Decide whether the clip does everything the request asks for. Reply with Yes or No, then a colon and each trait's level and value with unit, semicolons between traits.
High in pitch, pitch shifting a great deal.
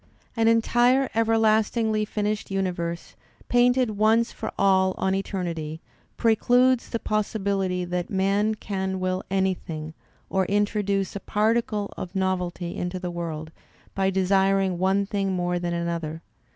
No: high, 195 Hz; average, 3.0 semitones